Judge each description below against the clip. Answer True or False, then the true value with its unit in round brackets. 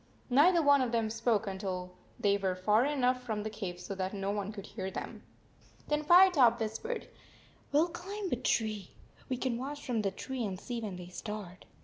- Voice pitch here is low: False (225 Hz)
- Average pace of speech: False (210 wpm)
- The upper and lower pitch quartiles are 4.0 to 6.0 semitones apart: True (5.1 semitones)